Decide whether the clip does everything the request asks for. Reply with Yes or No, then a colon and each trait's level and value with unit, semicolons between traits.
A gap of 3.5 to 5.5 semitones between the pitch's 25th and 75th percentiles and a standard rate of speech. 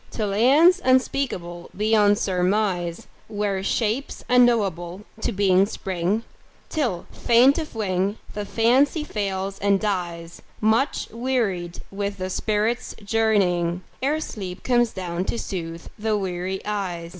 No: average, 4.0 semitones; slow, 120 wpm